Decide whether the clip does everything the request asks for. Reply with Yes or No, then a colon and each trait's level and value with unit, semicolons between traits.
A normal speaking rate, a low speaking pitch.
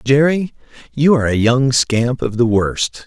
Yes: average, 175 wpm; low, 125 Hz